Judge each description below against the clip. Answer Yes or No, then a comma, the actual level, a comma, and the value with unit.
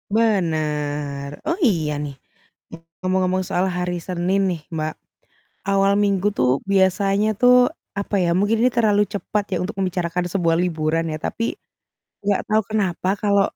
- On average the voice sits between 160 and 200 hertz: Yes, medium, 185 Hz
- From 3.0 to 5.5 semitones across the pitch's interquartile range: Yes, average, 3.7 semitones